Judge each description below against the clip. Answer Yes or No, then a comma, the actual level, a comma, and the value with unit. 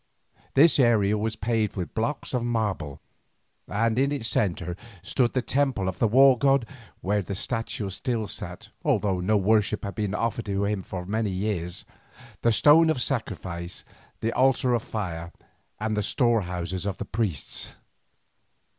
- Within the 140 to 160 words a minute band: Yes, average, 155 wpm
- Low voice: Yes, low, 110 Hz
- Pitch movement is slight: No, average, 3.8 semitones